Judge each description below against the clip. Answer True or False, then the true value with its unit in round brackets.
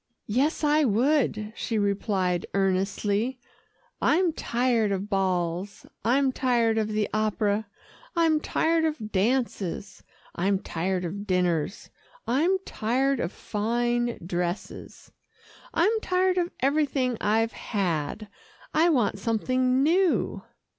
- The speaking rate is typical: False (110 wpm)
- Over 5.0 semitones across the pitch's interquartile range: True (5.5 semitones)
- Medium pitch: False (225 Hz)